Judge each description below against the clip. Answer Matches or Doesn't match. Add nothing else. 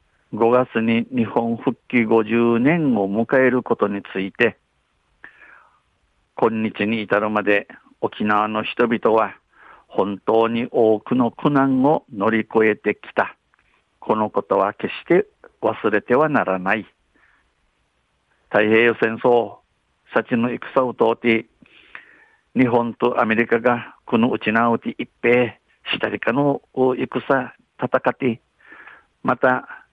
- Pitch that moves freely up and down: Doesn't match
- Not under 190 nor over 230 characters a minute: Matches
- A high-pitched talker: Doesn't match